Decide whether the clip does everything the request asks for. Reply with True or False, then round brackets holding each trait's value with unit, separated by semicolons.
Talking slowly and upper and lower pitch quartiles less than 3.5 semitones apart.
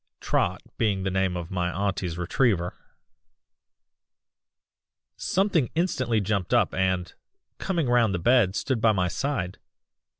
False (125 wpm; 5.3 semitones)